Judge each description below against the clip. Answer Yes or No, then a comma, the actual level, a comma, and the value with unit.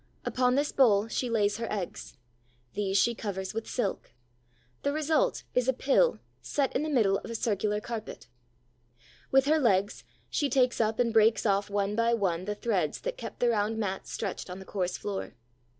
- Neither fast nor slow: Yes, average, 185 wpm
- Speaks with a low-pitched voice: No, high, 220 Hz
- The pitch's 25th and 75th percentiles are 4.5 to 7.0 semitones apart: No, average, 4.0 semitones